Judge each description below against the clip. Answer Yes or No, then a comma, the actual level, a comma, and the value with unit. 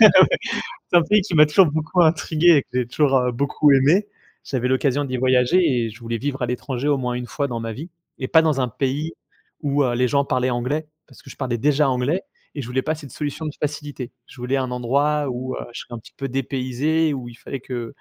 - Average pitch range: Yes, average, 3.2 semitones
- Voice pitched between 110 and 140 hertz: Yes, low, 135 Hz